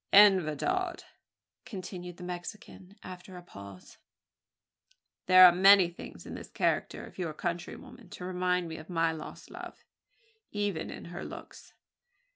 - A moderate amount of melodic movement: No, narrow, 2.2 semitones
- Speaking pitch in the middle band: Yes, medium, 180 Hz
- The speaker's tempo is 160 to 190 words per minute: No, average, 140 wpm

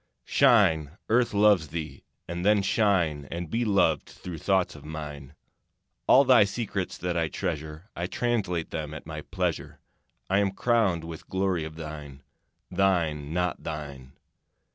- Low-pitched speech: Yes, very low, 85 Hz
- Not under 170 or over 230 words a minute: No, average, 145 wpm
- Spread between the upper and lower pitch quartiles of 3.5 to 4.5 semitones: Yes, average, 4.2 semitones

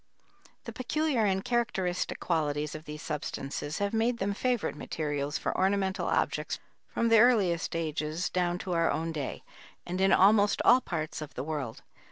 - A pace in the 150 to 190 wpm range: Yes, average, 165 wpm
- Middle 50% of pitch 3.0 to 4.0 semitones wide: No, average, 5.2 semitones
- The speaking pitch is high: No, medium, 180 Hz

